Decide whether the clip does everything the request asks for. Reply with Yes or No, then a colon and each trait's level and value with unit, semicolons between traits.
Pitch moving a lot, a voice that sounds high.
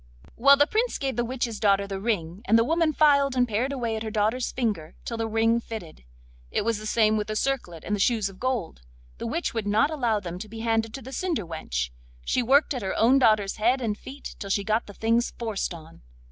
No: average, 3.7 semitones; high, 225 Hz